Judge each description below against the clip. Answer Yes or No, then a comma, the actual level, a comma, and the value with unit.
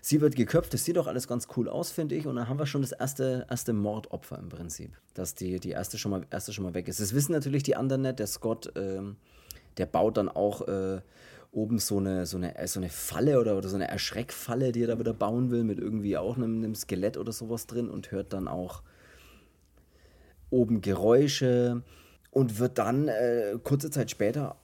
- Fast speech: Yes, fast, 215 wpm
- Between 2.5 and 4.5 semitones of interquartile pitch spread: No, average, 5.3 semitones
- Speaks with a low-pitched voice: Yes, low, 110 Hz